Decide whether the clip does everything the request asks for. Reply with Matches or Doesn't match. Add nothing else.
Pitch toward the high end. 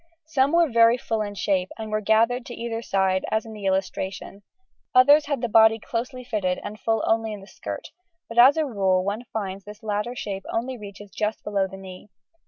Matches